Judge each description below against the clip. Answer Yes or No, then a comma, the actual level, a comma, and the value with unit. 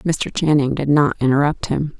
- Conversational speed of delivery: Yes, average, 180 wpm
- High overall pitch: No, medium, 145 Hz